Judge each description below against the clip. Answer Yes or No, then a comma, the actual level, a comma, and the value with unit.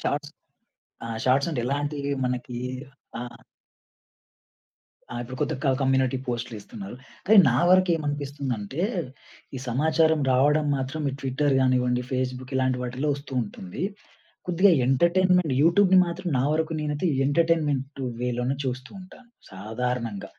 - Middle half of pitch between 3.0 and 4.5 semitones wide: Yes, average, 3.9 semitones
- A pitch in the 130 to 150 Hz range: Yes, low, 135 Hz